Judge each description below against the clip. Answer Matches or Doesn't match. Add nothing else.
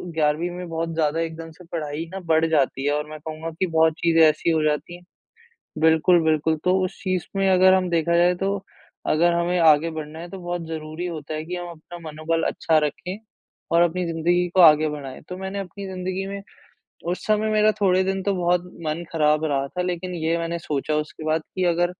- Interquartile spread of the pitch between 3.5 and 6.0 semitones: Doesn't match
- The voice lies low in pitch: Doesn't match